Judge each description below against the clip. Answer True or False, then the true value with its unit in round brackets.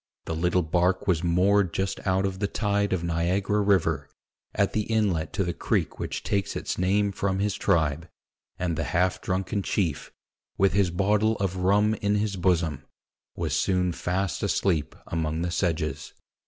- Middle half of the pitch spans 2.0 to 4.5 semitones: True (2.8 semitones)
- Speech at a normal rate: True (170 wpm)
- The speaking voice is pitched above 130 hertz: False (95 Hz)